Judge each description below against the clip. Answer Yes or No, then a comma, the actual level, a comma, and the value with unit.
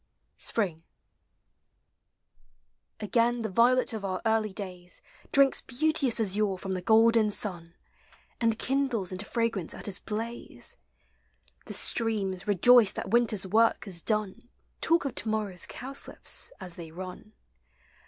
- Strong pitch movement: No, average, 3.7 semitones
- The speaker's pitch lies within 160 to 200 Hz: No, high, 215 Hz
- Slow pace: Yes, slow, 125 wpm